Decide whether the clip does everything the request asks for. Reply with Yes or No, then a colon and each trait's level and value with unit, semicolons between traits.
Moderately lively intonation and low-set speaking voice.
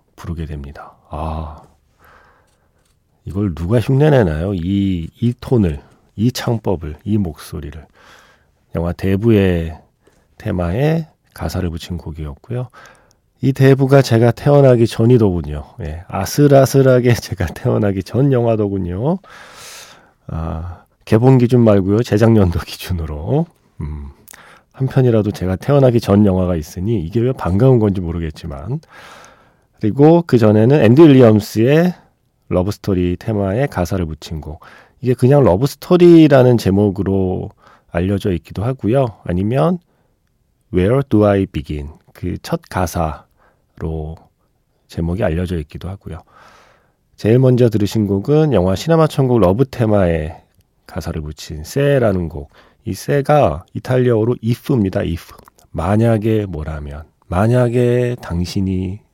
No: wide, 6.2 semitones; low, 105 Hz